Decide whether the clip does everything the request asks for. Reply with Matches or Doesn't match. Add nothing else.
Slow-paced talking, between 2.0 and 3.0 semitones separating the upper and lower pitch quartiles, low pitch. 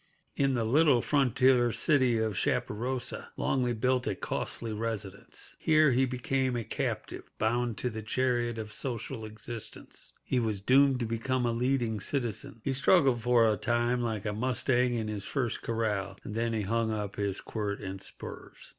Doesn't match